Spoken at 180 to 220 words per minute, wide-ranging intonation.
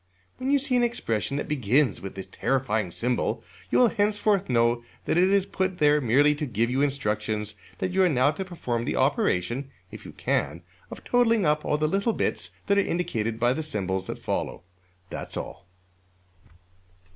Yes: average, 185 wpm; wide, 8.4 semitones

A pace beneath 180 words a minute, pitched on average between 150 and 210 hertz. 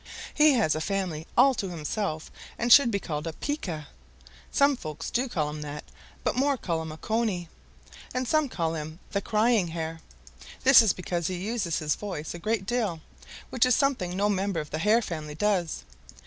No: average, 190 wpm; medium, 185 Hz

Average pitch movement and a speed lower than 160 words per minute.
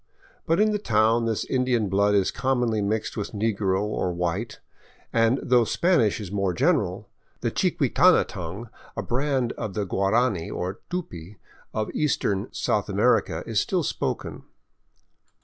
Yes: average, 4.2 semitones; average, 145 wpm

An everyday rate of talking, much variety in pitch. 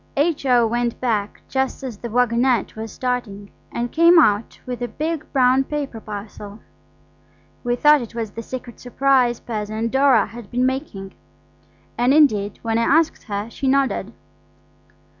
No: average, 150 wpm; average, 3.3 semitones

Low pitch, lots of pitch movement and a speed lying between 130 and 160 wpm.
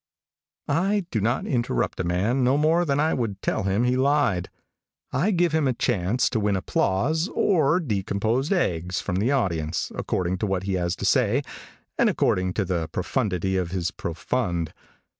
No: low, 105 Hz; wide, 7.1 semitones; average, 175 wpm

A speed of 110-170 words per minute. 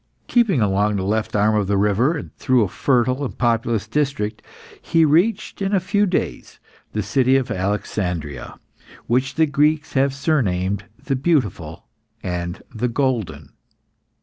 Yes: average, 150 wpm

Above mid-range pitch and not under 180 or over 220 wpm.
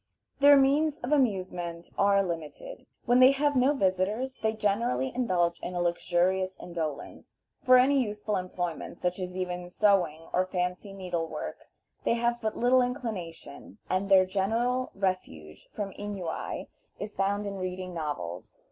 No: high, 195 Hz; average, 145 wpm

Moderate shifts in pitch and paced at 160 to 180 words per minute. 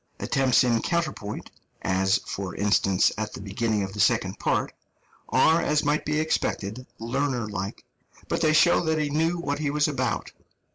No: wide, 7.0 semitones; average, 170 wpm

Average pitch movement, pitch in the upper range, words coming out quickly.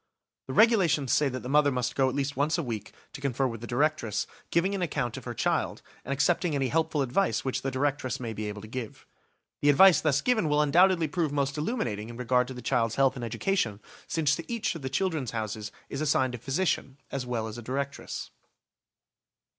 No: average, 4.0 semitones; low, 135 Hz; fast, 215 wpm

